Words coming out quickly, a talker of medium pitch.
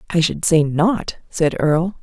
No: average, 180 wpm; medium, 165 Hz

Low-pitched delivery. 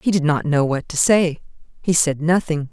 No: medium, 160 Hz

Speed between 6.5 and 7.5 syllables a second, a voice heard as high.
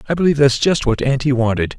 No: 6.8 syllables/s; low, 135 Hz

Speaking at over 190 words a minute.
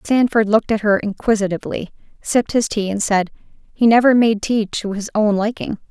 No: average, 185 wpm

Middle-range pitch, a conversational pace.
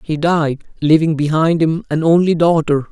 Yes: medium, 160 Hz; average, 165 wpm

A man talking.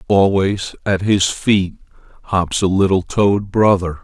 Yes: male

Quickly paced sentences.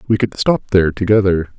No: average, 190 wpm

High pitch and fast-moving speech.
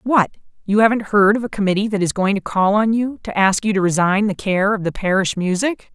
Yes: high, 205 Hz; fast, 250 wpm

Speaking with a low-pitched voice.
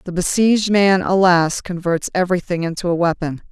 No: medium, 180 Hz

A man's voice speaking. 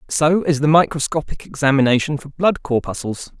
Yes: male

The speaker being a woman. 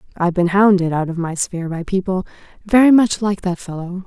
Yes: female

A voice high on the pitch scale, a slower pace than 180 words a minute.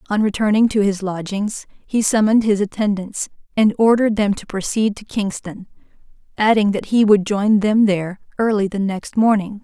Yes: high, 205 Hz; average, 170 wpm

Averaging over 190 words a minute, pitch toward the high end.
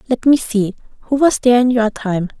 Yes: average, 200 wpm; high, 235 Hz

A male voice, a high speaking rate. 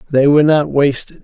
No: male; average, 195 wpm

